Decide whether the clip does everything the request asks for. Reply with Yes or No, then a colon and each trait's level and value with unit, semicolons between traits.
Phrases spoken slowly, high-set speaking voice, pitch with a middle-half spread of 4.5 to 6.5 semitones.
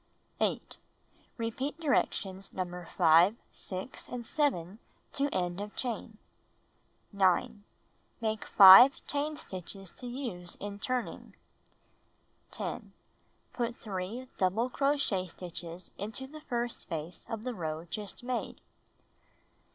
Yes: slow, 110 wpm; high, 210 Hz; average, 5.3 semitones